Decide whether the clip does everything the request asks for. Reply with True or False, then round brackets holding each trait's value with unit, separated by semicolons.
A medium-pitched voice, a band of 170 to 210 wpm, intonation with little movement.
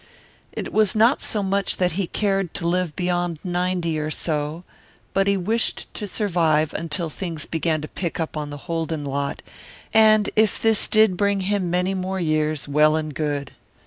False (175 Hz; 175 wpm; 3.9 semitones)